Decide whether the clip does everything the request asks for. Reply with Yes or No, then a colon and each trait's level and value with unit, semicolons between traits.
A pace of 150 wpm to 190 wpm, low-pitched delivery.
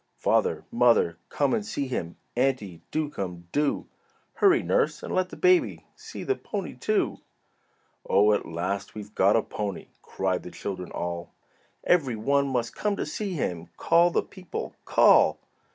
Yes: average, 160 wpm; low, 130 Hz